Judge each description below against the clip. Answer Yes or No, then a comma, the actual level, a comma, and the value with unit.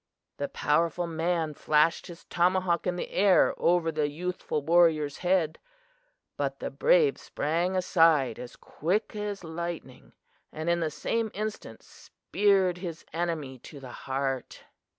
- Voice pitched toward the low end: No, medium, 170 Hz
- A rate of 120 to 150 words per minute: Yes, slow, 135 wpm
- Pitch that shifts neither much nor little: Yes, average, 3.1 semitones